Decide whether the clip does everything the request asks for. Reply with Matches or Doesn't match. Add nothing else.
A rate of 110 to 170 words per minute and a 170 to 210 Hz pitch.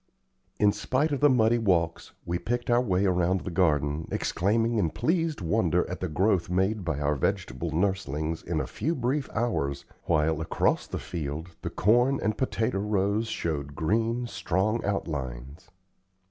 Doesn't match